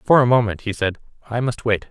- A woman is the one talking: No, male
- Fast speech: Yes, fast, 250 wpm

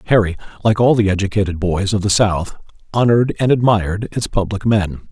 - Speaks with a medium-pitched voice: No, low, 100 Hz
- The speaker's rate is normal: Yes, average, 175 wpm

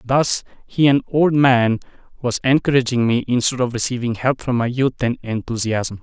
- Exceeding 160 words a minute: Yes, average, 170 wpm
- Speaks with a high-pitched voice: No, low, 125 Hz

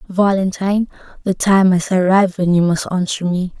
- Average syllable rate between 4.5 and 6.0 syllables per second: Yes, 5.3 syllables/s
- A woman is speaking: Yes, female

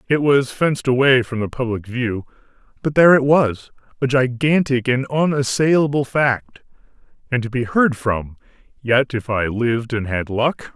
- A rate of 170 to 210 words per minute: No, average, 155 wpm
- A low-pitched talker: Yes, low, 125 Hz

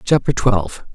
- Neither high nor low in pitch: No, low, 110 Hz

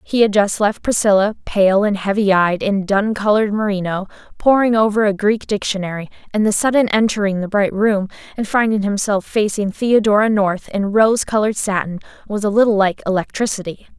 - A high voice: Yes, high, 205 Hz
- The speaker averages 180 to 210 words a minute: No, average, 170 wpm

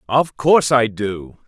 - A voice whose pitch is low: Yes, low, 120 Hz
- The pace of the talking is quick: No, average, 160 wpm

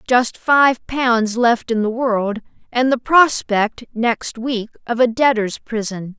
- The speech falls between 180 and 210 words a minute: No, average, 145 wpm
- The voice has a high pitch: Yes, high, 235 Hz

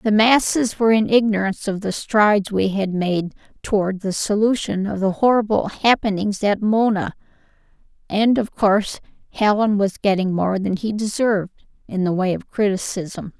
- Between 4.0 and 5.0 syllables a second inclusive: Yes, 4.9 syllables/s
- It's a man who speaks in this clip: No, female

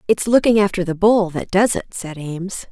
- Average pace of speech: No, fast, 220 wpm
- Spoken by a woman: Yes, female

